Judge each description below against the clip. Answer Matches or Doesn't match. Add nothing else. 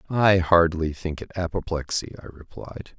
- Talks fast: Doesn't match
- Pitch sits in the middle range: Doesn't match